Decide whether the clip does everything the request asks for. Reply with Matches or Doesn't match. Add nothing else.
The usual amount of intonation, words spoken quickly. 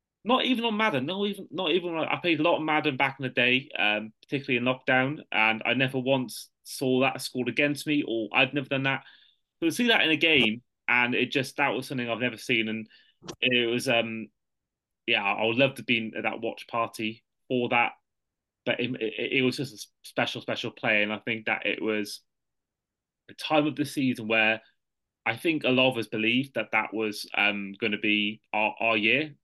Matches